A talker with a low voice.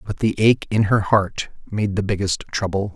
Yes: low, 100 Hz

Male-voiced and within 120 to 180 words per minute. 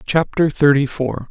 Yes: male; average, 140 wpm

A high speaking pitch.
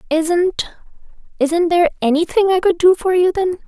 Yes: very high, 345 Hz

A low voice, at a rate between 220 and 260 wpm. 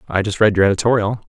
Yes: low, 105 Hz; fast, 230 wpm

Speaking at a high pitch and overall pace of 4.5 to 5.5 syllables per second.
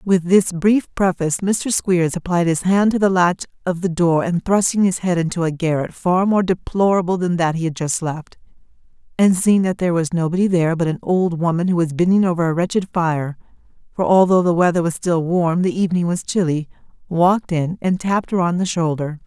No: medium, 175 Hz; 4.7 syllables/s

